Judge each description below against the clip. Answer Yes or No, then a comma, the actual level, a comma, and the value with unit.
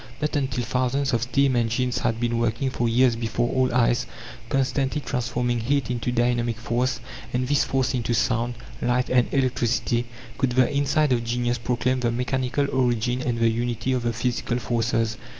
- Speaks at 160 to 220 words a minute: Yes, average, 170 wpm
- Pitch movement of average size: No, narrow, 1.6 semitones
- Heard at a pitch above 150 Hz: No, low, 125 Hz